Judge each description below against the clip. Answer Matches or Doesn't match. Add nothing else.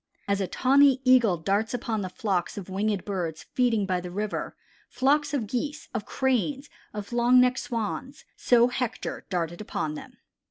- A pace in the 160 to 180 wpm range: Matches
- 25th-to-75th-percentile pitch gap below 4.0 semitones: Doesn't match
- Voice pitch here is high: Matches